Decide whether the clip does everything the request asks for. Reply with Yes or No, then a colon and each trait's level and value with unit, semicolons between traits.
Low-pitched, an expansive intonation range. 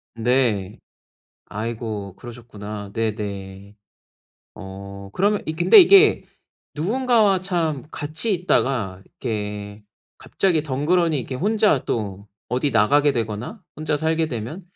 Yes: low, 125 Hz; wide, 7.8 semitones